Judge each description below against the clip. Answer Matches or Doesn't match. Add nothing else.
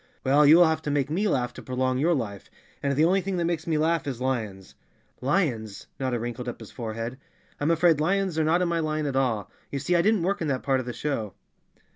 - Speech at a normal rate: Doesn't match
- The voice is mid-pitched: Matches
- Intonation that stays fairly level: Doesn't match